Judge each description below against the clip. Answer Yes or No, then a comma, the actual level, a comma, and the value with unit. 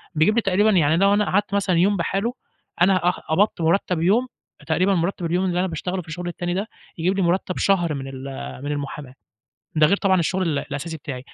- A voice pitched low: No, medium, 180 Hz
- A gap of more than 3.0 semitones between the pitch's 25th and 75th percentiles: Yes, average, 3.4 semitones